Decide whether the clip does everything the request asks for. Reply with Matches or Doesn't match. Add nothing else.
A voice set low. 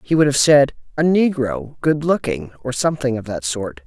Matches